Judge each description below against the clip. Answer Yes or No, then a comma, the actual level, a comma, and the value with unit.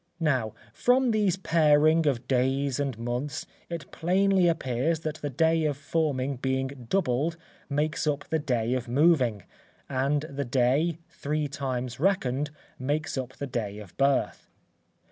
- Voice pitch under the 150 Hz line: Yes, medium, 140 Hz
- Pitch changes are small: No, average, 3.8 semitones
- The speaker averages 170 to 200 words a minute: No, average, 145 wpm